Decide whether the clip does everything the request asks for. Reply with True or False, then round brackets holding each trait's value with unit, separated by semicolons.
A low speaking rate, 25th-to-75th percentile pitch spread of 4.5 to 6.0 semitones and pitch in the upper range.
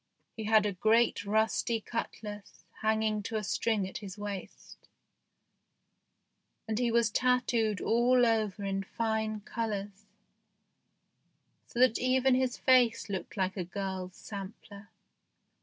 False (125 wpm; 2.4 semitones; 215 Hz)